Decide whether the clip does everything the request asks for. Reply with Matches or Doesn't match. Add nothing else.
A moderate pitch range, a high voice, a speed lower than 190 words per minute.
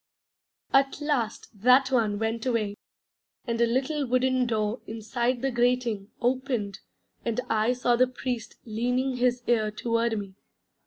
Doesn't match